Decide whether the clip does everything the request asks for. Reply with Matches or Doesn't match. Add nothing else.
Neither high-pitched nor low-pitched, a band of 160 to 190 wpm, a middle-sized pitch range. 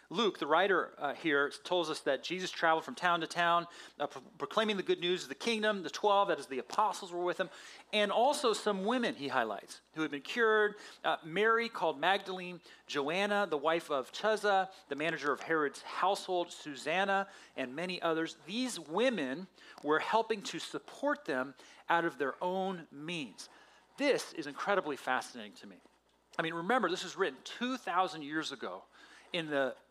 Matches